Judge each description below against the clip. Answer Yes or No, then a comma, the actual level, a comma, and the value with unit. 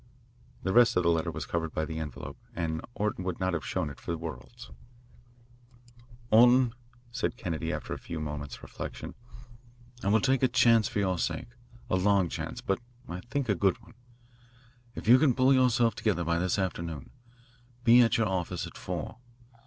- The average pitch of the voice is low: Yes, very low, 95 Hz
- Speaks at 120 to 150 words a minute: No, average, 185 wpm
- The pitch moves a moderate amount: No, wide, 5.8 semitones